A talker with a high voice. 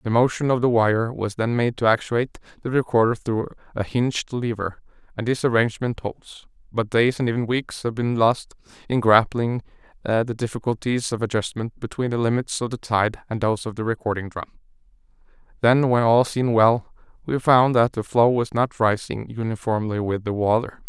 No: low, 115 Hz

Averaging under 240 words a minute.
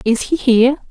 Yes: average, 200 wpm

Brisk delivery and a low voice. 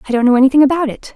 No: fast, 315 wpm; very high, 265 Hz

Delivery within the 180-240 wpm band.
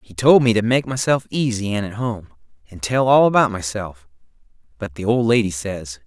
Yes: average, 200 wpm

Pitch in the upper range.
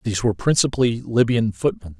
No: low, 115 Hz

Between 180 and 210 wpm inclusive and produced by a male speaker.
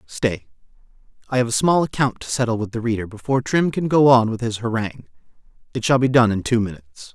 Yes: average, 200 wpm; male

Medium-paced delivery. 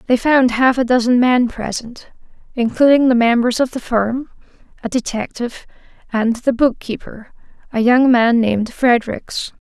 Yes: average, 145 wpm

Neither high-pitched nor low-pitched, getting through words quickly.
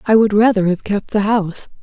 No: high, 205 Hz; fast, 230 wpm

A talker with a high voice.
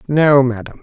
No: low, 135 Hz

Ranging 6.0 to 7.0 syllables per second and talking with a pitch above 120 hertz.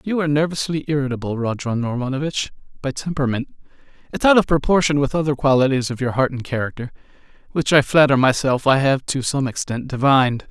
Yes: 6.2 syllables/s; low, 135 Hz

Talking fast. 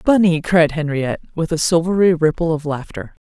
No: average, 165 wpm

